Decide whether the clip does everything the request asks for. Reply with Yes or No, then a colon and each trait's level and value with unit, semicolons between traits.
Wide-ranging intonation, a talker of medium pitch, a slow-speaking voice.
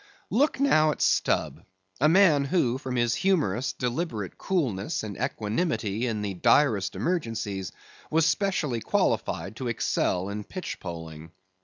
No: wide, 7.9 semitones; low, 120 Hz; slow, 130 wpm